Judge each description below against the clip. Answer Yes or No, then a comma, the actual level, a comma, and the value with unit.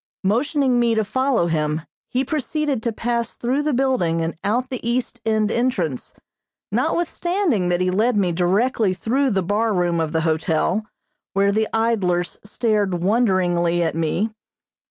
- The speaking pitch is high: Yes, high, 215 Hz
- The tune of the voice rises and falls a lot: Yes, wide, 5.8 semitones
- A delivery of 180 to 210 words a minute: No, average, 155 wpm